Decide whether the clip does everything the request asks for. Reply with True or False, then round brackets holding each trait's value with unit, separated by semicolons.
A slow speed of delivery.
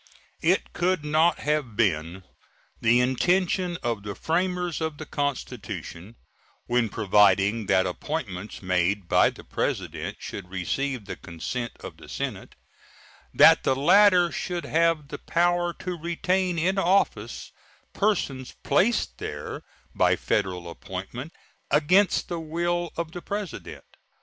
True (125 wpm)